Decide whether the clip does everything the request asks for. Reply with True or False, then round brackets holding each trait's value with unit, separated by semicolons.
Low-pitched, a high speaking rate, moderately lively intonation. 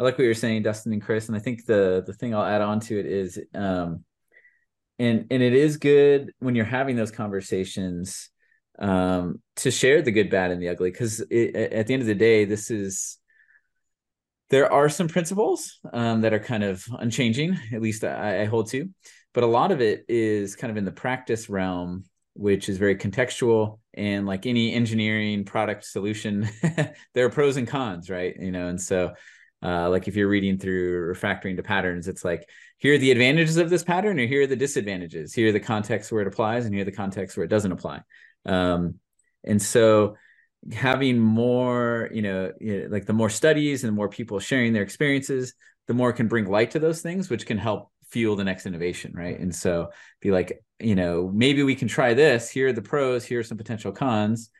True (110 Hz; 210 wpm; 4.2 semitones)